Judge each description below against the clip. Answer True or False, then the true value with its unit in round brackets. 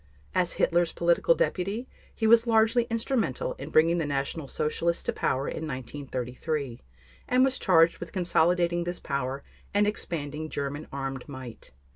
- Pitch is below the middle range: False (165 Hz)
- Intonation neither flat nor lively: False (6.6 semitones)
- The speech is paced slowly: False (145 wpm)